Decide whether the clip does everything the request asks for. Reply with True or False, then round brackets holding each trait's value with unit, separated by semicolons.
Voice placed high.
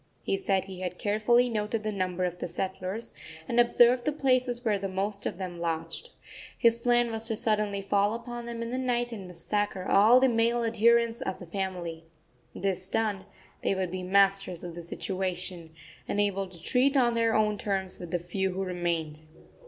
True (200 Hz)